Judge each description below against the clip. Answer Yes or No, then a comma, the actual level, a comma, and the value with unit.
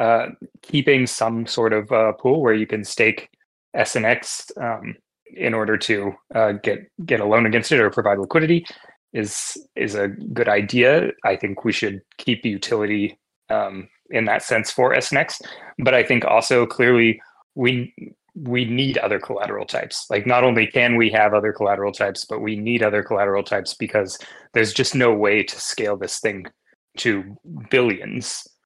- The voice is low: Yes, low, 110 Hz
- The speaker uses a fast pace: No, average, 170 wpm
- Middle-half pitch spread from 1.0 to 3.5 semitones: Yes, average, 2.8 semitones